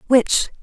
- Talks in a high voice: Yes, high, 245 Hz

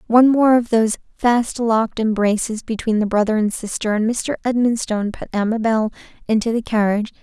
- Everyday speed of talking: Yes, average, 165 wpm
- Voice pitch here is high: Yes, high, 225 Hz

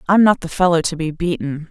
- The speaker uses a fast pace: Yes, fast, 245 wpm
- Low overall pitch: No, medium, 170 Hz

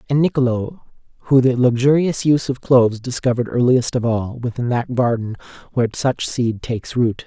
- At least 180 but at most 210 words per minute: No, average, 165 wpm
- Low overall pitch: Yes, low, 125 Hz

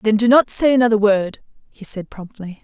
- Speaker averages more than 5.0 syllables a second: Yes, 5.3 syllables/s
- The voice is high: Yes, high, 215 Hz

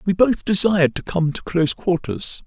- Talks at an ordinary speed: Yes, average, 195 wpm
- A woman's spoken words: No, male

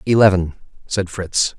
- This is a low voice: Yes, very low, 95 Hz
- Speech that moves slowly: Yes, slow, 115 wpm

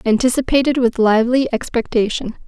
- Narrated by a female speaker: Yes, female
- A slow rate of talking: Yes, slow, 95 wpm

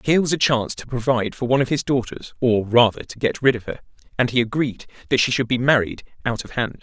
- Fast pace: Yes, fast, 255 wpm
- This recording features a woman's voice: No, male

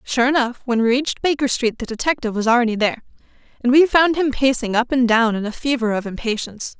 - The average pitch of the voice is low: No, high, 245 Hz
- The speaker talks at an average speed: No, fast, 220 wpm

